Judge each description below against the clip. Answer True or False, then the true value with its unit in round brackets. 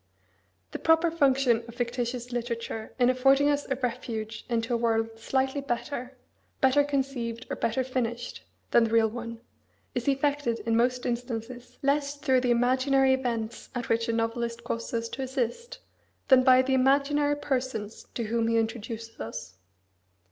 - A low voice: False (245 Hz)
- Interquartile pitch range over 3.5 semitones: False (2.5 semitones)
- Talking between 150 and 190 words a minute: True (155 wpm)